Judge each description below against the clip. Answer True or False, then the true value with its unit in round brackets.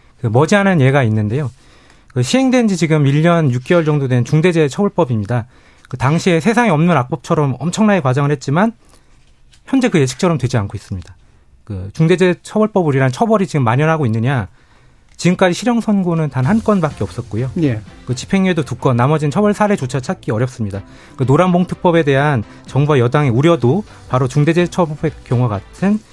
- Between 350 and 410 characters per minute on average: True (390 characters per minute)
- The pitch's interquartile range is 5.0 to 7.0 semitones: True (6.3 semitones)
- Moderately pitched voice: True (150 Hz)